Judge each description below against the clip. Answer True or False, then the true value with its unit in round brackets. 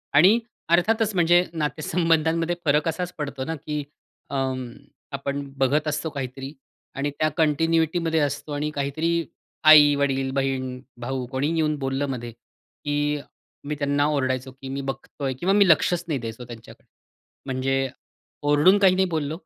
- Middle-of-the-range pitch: True (145 Hz)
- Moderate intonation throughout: True (3.2 semitones)